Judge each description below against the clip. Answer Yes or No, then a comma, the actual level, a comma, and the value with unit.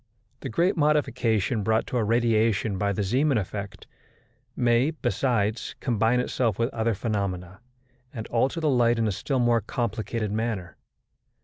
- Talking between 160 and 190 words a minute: No, average, 145 wpm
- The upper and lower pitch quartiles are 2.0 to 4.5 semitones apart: Yes, average, 3.0 semitones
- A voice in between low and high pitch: No, low, 115 Hz